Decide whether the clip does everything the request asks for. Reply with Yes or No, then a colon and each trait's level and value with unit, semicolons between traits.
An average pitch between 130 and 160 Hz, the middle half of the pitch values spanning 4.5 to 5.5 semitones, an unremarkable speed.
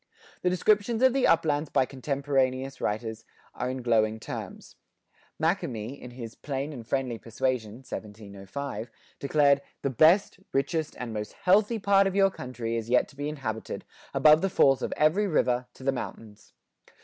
Yes: low, 135 Hz; average, 5.2 semitones; average, 160 wpm